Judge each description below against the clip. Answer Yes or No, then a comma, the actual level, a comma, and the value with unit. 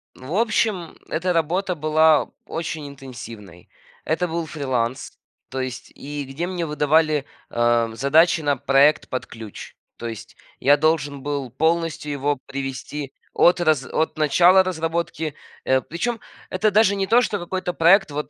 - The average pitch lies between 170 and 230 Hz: No, medium, 155 Hz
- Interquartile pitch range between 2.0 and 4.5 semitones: Yes, average, 4.0 semitones